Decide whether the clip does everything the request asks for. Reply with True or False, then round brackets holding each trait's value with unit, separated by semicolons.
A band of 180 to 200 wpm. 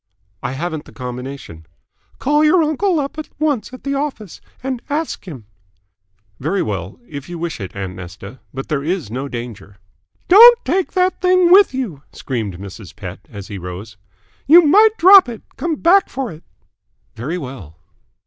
False (170 wpm)